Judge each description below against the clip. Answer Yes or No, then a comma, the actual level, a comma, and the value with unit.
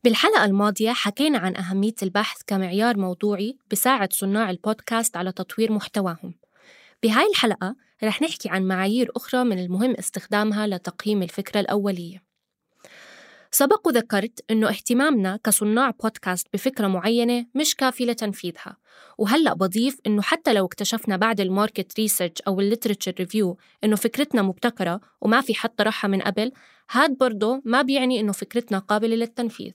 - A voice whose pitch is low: No, high, 215 Hz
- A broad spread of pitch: No, average, 3.5 semitones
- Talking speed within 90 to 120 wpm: No, fast, 135 wpm